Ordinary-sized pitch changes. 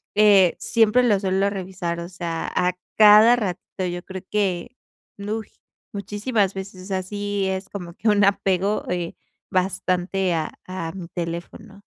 No: narrow, 2.3 semitones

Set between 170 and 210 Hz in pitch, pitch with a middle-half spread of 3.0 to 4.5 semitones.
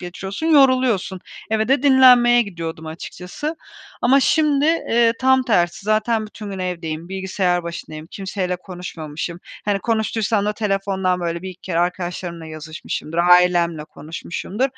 No: high, 190 Hz; average, 4.9 semitones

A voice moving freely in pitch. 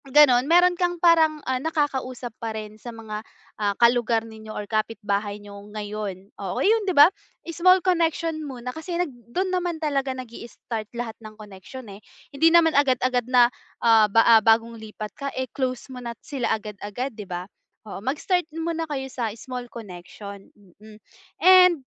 Yes: wide, 6.5 semitones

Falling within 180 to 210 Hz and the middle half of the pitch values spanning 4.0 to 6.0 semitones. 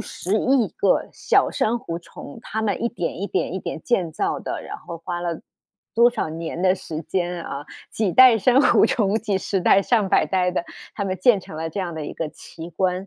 Yes: medium, 185 Hz; average, 4.5 semitones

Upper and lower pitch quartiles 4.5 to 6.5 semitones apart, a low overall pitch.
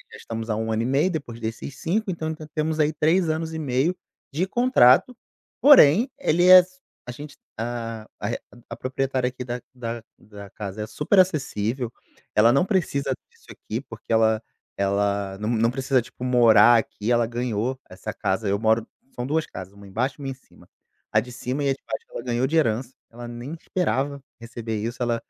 Yes: average, 5.0 semitones; low, 125 Hz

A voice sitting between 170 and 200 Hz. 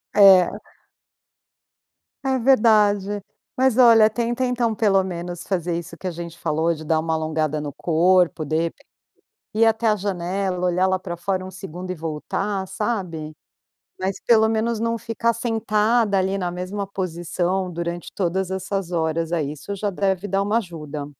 Yes: high, 190 Hz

